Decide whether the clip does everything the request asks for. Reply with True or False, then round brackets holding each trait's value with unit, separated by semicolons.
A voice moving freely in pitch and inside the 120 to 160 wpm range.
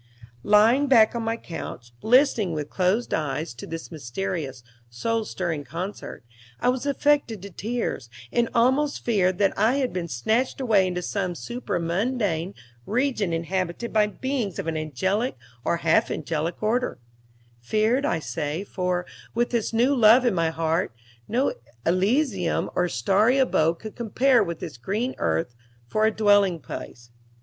True (6.1 semitones; 150 wpm)